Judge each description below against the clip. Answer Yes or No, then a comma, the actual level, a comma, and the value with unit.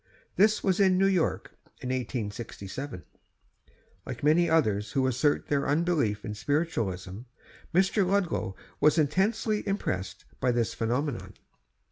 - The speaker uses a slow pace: Yes, slow, 120 wpm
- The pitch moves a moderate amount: No, wide, 8.2 semitones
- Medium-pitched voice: Yes, medium, 145 Hz